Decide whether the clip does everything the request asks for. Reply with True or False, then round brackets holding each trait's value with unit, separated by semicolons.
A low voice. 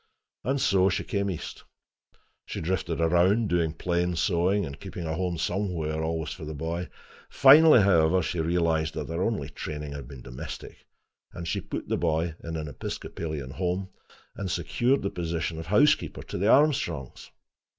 True (85 Hz)